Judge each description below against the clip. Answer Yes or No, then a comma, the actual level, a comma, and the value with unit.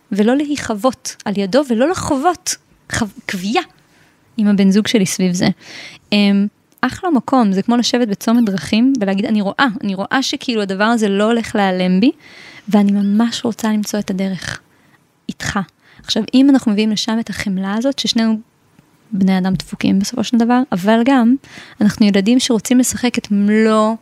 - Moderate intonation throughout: Yes, average, 3.3 semitones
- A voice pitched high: Yes, high, 220 Hz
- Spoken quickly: Yes, fast, 160 wpm